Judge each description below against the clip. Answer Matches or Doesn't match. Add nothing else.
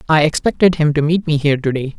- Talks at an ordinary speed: Doesn't match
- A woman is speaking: Doesn't match